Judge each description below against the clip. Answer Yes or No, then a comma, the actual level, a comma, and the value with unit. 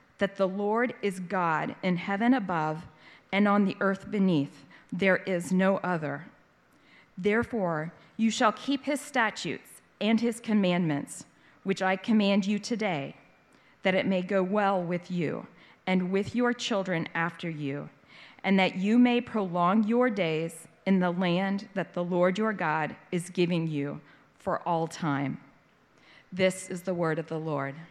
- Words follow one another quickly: No, average, 155 wpm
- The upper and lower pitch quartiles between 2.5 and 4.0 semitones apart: Yes, average, 3.5 semitones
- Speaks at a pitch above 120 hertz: Yes, medium, 185 Hz